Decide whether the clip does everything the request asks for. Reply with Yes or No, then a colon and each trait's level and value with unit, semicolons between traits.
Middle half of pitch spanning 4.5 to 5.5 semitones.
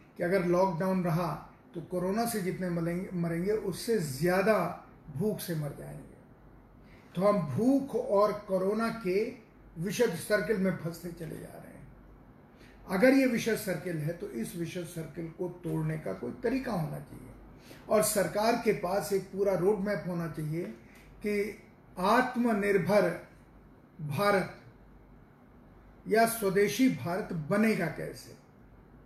No: average, 3.5 semitones